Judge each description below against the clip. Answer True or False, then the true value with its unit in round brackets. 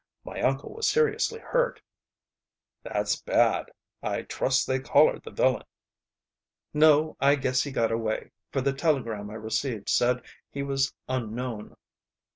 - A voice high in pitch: False (135 Hz)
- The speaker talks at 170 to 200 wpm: False (135 wpm)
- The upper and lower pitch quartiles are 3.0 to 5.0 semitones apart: True (4.2 semitones)